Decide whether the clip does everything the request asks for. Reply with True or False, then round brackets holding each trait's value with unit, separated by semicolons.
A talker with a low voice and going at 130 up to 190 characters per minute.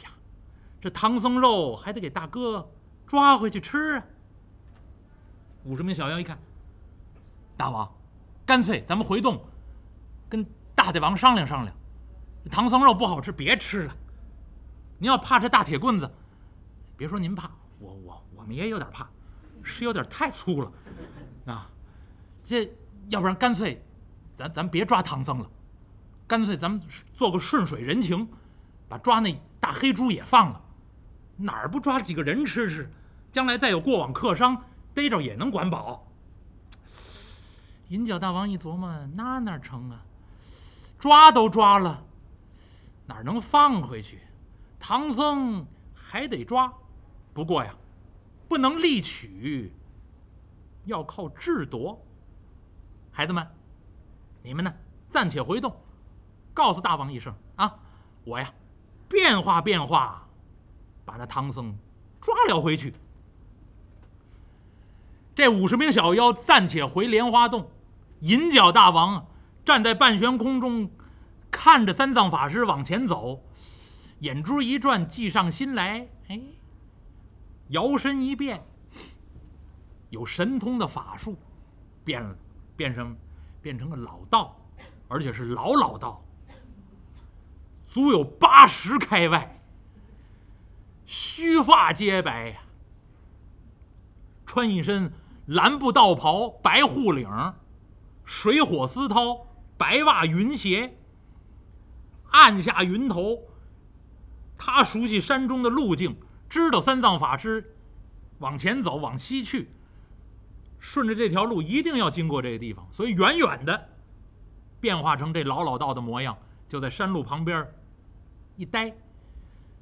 True (130 Hz; 175 characters per minute)